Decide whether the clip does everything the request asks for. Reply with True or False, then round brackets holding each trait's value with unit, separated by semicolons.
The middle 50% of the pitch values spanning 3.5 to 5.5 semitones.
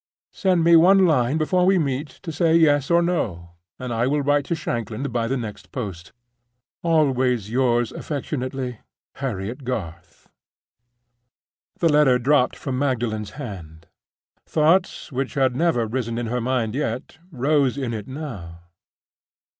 True (4.6 semitones)